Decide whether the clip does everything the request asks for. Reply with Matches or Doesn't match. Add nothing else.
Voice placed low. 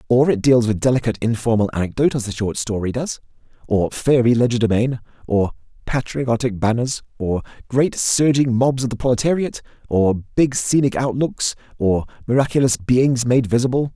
Matches